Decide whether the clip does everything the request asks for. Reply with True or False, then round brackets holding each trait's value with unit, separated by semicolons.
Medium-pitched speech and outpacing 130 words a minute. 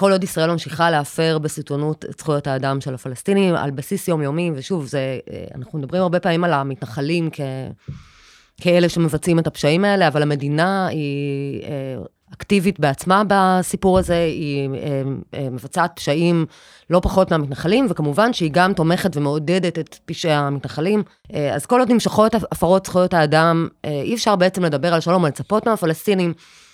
True (165 Hz; 145 wpm)